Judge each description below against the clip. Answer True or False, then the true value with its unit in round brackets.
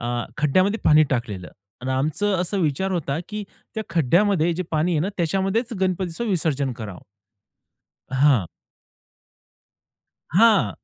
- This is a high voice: False (165 Hz)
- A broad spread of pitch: True (6.3 semitones)